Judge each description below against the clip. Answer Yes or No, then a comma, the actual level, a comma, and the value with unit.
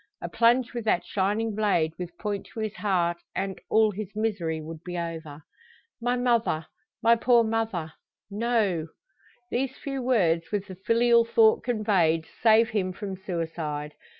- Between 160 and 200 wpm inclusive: No, average, 150 wpm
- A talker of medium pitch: No, high, 205 Hz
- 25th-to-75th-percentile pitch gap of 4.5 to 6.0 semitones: Yes, average, 5.2 semitones